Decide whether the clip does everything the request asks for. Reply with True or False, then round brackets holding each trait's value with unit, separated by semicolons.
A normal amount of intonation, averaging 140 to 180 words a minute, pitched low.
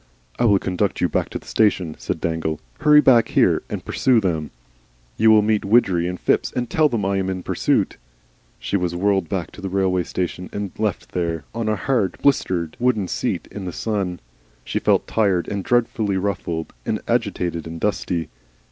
False (3.6 semitones; 190 wpm; 95 Hz)